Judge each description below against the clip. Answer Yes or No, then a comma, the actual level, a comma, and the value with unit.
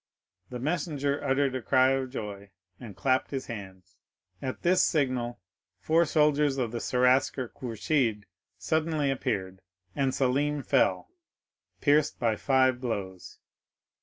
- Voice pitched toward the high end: No, low, 130 Hz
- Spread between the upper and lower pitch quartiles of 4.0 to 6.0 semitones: No, average, 3.4 semitones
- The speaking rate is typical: No, slow, 125 wpm